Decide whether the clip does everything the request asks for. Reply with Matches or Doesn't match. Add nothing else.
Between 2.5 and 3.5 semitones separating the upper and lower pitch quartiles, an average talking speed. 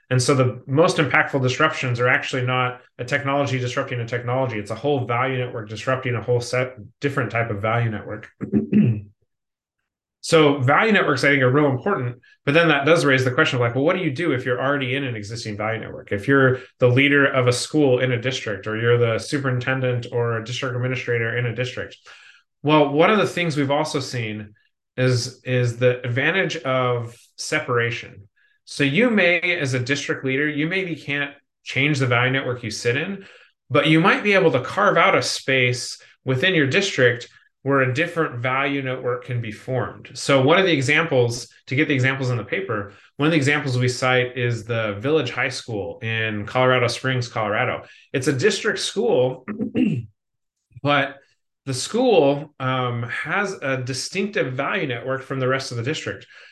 Matches